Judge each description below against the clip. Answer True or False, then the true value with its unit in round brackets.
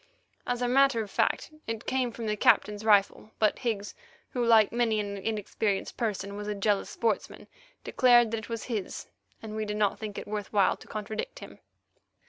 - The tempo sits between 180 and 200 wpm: True (190 wpm)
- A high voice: True (215 Hz)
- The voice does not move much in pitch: True (2.0 semitones)